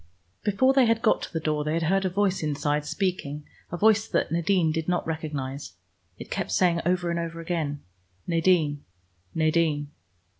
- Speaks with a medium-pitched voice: Yes, medium, 165 Hz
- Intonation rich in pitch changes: No, average, 3.5 semitones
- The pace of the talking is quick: No, average, 175 wpm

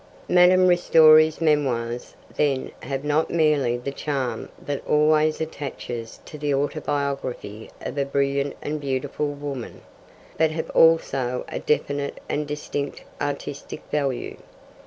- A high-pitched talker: No, medium, 145 Hz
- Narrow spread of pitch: Yes, narrow, 2.0 semitones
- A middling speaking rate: No, slow, 120 wpm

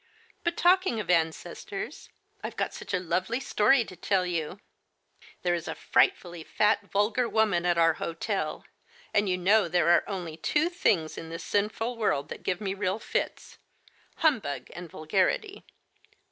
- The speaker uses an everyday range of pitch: Yes, average, 4.6 semitones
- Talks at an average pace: Yes, average, 160 wpm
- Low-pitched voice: No, high, 190 Hz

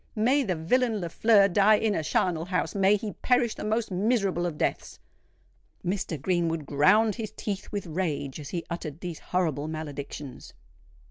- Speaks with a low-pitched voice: No, medium, 185 Hz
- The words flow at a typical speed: Yes, average, 155 wpm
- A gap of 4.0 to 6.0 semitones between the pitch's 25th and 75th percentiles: Yes, average, 5.0 semitones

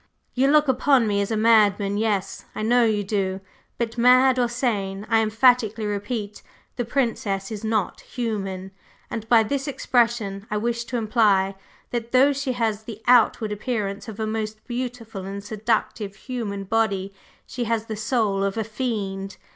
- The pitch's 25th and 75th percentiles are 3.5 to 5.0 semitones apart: No, average, 3.0 semitones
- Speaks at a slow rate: No, average, 165 wpm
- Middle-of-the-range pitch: No, high, 220 Hz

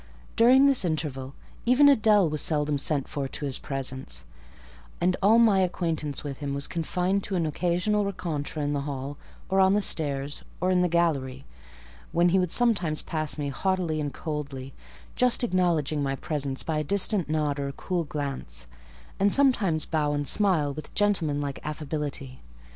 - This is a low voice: No, medium, 155 Hz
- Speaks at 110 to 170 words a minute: Yes, average, 165 wpm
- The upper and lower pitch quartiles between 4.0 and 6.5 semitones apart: Yes, average, 4.6 semitones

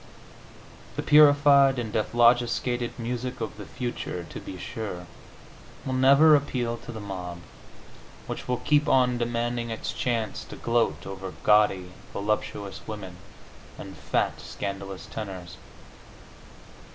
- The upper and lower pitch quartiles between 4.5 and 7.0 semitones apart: No, average, 3.9 semitones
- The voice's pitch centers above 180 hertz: No, low, 115 Hz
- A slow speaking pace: Yes, slow, 120 wpm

